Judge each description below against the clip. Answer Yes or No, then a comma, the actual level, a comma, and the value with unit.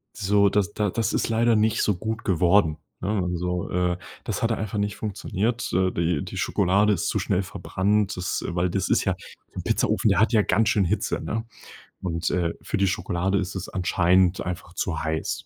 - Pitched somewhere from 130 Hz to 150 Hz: No, very low, 95 Hz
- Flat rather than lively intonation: No, average, 3.0 semitones